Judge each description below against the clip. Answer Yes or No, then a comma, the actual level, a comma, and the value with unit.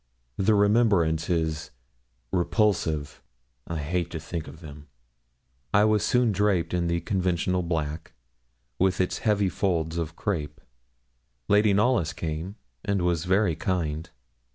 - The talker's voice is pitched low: Yes, very low, 90 Hz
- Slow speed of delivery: Yes, slow, 130 wpm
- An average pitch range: Yes, average, 3.9 semitones